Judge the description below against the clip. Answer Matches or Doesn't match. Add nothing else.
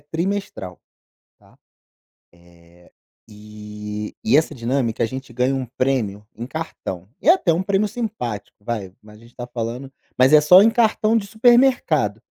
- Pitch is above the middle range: Doesn't match